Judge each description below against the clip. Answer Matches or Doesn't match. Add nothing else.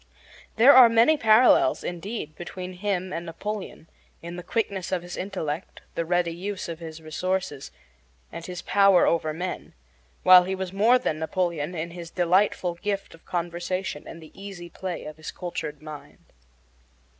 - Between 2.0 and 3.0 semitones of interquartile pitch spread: Matches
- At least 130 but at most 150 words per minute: Doesn't match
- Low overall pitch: Doesn't match